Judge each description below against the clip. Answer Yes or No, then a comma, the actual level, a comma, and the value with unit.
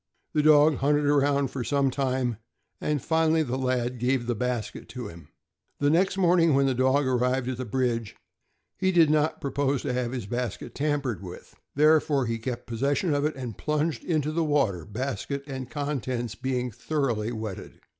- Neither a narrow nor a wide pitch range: Yes, average, 3.2 semitones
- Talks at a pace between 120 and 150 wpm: No, average, 175 wpm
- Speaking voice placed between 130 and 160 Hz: Yes, low, 135 Hz